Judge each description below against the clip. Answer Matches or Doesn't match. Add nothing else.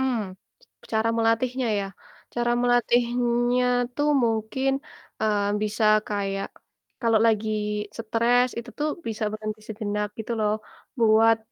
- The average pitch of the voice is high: Matches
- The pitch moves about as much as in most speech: Doesn't match